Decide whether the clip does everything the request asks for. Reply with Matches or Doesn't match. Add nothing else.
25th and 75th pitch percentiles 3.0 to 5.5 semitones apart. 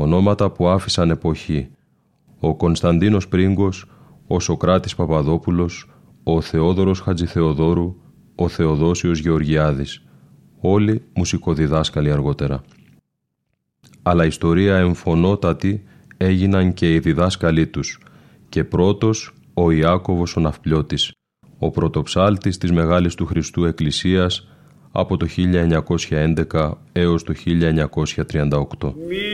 Doesn't match